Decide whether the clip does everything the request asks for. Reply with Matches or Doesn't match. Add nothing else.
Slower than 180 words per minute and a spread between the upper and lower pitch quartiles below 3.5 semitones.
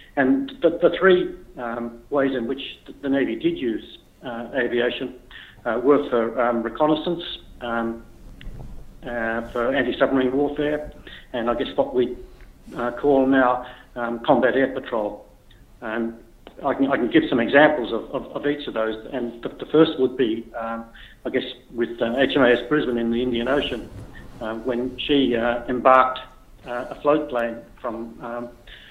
Matches